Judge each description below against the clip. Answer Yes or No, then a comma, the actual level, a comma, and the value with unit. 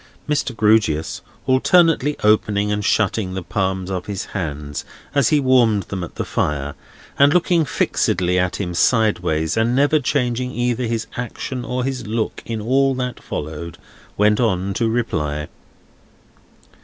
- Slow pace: No, average, 145 wpm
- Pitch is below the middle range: Yes, low, 110 Hz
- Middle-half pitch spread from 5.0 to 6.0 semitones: Yes, wide, 5.6 semitones